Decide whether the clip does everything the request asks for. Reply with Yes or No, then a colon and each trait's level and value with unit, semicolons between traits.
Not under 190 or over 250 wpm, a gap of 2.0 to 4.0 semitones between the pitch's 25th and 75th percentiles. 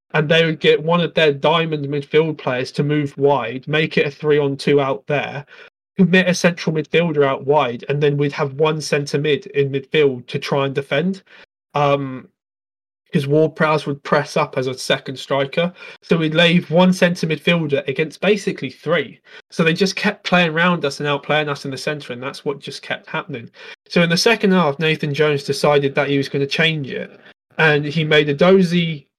Yes: average, 200 wpm; average, 3.0 semitones